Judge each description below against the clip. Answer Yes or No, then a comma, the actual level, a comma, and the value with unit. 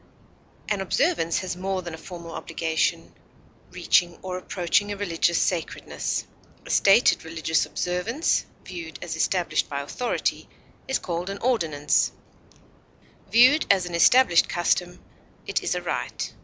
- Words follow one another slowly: Yes, slow, 130 wpm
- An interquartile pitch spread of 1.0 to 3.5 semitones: Yes, average, 3.1 semitones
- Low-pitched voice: No, medium, 180 Hz